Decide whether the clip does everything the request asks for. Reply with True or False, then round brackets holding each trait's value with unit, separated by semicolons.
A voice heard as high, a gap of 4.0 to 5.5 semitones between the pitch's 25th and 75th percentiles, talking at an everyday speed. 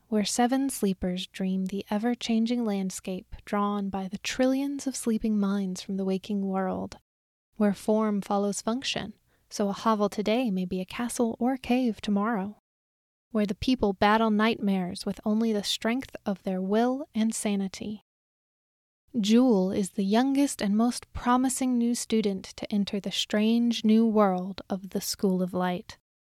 False (210 Hz; 2.9 semitones; 155 wpm)